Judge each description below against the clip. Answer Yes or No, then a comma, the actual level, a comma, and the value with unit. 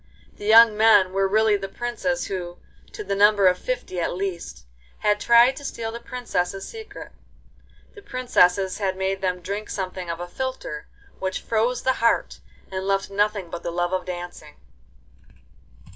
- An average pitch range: Yes, average, 4.0 semitones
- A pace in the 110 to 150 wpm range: No, average, 165 wpm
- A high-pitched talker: Yes, high, 195 Hz